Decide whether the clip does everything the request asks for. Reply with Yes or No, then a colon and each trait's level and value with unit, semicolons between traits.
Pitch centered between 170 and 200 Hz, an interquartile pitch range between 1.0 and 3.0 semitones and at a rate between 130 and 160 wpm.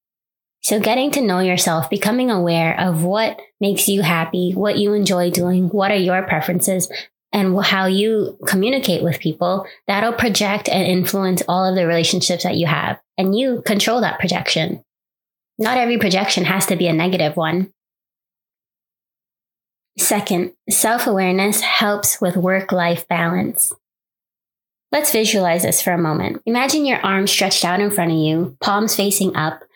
Yes: high, 190 Hz; average, 2.7 semitones; average, 155 wpm